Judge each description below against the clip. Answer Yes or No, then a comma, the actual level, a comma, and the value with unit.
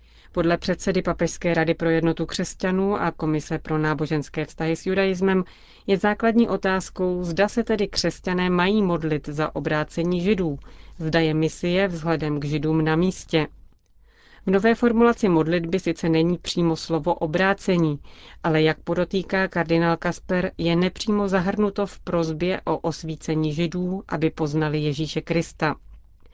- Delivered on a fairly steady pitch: No, average, 3.1 semitones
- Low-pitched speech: No, medium, 170 Hz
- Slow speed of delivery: No, average, 135 wpm